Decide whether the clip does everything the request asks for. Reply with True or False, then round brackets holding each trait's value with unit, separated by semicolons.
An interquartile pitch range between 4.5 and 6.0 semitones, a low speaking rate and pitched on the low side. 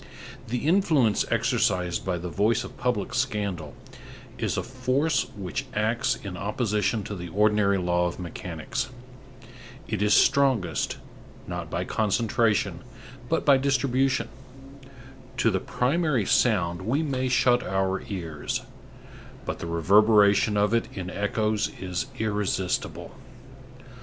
True (4.9 semitones; 120 wpm; 105 Hz)